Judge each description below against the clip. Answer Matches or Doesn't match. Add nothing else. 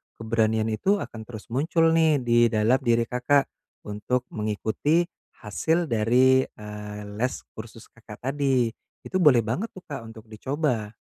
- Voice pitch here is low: Matches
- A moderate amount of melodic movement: Matches